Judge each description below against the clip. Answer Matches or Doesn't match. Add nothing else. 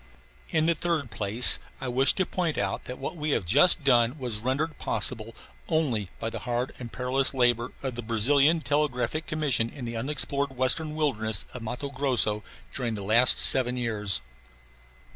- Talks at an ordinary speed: Matches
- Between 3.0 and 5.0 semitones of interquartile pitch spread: Matches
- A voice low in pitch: Matches